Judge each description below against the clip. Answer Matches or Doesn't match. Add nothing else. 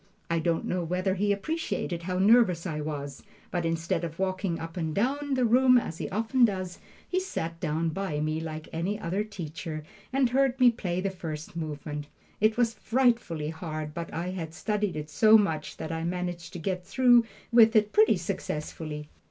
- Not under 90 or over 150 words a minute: Doesn't match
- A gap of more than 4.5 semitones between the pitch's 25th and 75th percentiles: Matches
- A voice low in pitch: Doesn't match